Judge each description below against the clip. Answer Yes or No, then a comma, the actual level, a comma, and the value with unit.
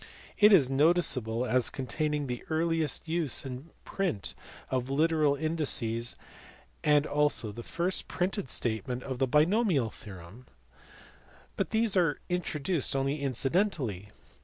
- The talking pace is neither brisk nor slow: No, slow, 125 wpm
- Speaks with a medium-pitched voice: Yes, medium, 145 Hz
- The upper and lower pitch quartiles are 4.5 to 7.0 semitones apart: Yes, average, 4.9 semitones